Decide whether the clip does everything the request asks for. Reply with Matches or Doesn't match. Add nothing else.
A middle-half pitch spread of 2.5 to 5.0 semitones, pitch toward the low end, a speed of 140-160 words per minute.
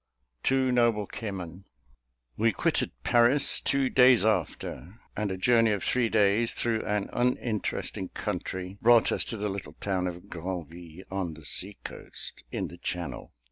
Matches